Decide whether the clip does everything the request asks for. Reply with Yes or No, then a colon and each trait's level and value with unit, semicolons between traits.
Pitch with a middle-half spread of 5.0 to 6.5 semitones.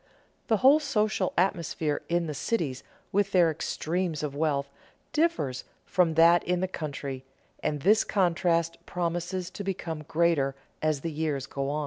No: average, 3.7 semitones